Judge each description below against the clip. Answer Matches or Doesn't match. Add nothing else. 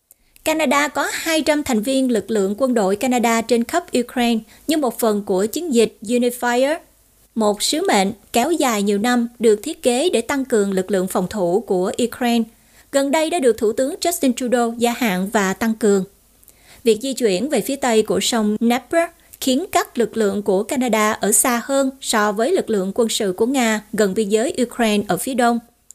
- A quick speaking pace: Doesn't match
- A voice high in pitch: Matches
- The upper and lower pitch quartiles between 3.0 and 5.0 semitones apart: Matches